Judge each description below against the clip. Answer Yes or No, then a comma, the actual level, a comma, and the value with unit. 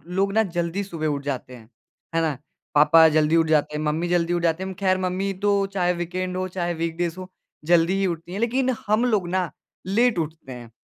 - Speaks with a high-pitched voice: No, medium, 175 Hz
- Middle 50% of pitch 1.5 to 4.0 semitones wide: Yes, average, 2.8 semitones